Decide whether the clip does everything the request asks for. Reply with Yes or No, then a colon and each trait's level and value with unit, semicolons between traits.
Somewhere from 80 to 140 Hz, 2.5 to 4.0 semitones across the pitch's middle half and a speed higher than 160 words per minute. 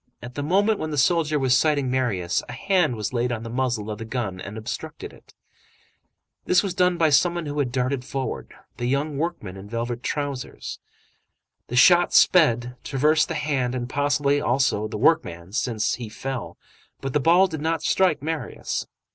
No: low, 135 Hz; average, 4.5 semitones; average, 180 wpm